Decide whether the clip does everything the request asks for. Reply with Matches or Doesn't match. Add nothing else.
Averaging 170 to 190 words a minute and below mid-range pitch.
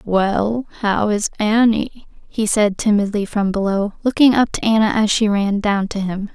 Doesn't match